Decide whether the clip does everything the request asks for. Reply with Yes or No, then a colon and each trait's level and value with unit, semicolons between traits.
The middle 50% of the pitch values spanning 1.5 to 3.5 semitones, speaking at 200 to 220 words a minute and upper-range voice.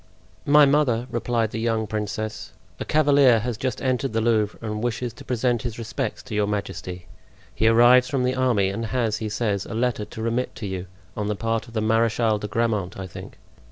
No: narrow, 2.5 semitones; fast, 205 wpm; low, 115 Hz